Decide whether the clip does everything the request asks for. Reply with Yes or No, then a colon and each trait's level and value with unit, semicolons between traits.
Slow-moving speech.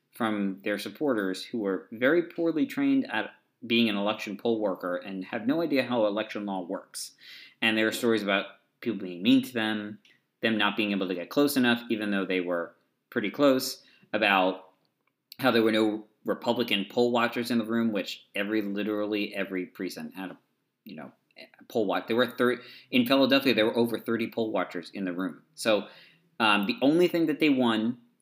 No: average, 195 wpm